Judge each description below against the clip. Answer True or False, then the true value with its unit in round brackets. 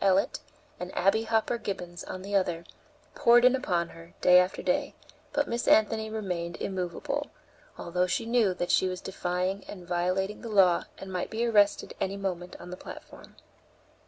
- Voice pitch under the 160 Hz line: False (190 Hz)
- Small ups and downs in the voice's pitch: False (3.5 semitones)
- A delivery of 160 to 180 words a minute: True (170 wpm)